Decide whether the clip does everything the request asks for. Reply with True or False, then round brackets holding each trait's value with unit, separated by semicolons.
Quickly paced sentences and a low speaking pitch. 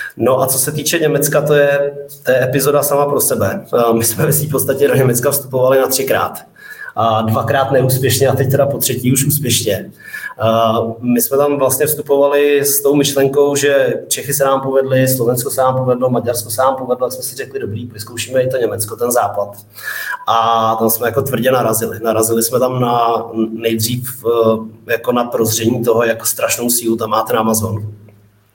True (185 wpm; 125 Hz)